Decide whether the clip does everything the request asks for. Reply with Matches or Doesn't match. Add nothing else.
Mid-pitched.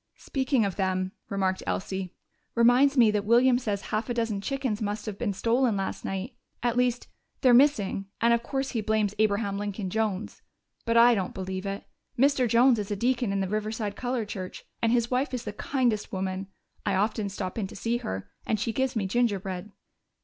Doesn't match